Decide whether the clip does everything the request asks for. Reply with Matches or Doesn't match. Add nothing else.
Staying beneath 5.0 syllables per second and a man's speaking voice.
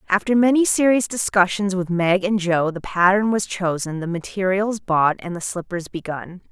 Doesn't match